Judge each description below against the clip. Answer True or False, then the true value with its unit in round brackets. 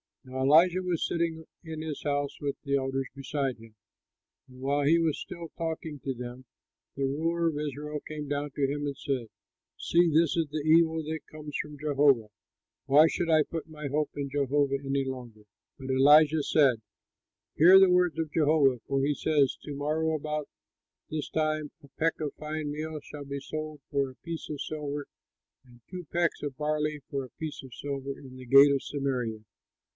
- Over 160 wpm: True (185 wpm)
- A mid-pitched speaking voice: True (145 Hz)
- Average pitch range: False (2.3 semitones)